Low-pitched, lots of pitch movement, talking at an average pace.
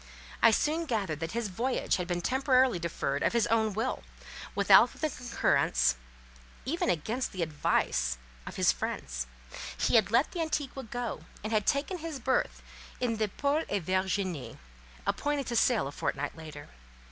No: high, 225 Hz; wide, 7.0 semitones; average, 160 wpm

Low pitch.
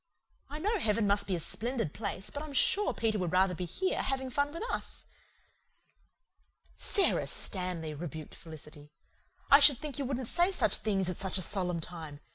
No: high, 205 Hz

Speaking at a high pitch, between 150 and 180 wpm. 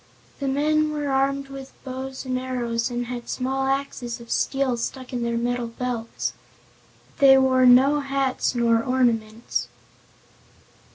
No: very high, 260 Hz; slow, 135 wpm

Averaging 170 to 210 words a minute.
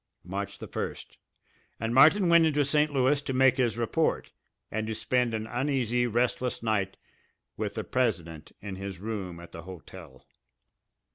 No: average, 155 wpm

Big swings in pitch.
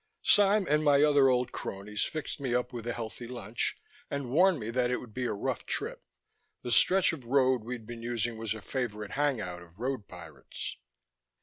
No: average, 4.0 semitones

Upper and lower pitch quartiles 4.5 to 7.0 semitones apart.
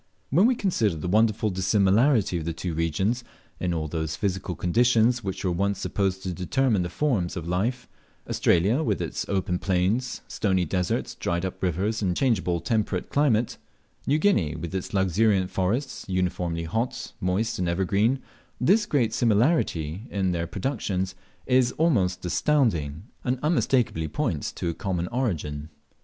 Yes: average, 5.2 semitones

